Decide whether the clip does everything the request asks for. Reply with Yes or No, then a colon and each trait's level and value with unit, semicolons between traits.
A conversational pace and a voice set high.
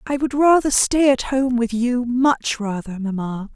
Yes: average, 170 wpm; high, 245 Hz